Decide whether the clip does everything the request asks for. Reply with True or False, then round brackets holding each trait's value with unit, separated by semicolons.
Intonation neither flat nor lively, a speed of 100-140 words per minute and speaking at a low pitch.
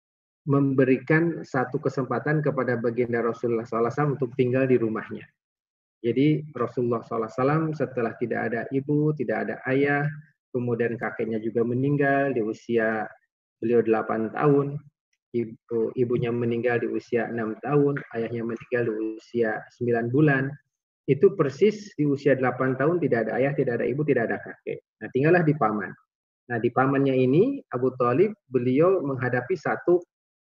True (3.5 semitones; 135 wpm; 130 Hz)